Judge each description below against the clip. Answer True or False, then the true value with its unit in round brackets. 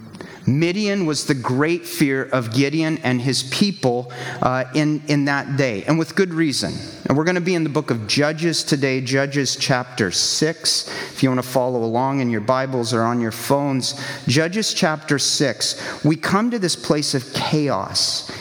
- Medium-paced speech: True (185 wpm)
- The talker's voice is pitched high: False (140 Hz)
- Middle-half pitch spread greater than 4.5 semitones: False (3.7 semitones)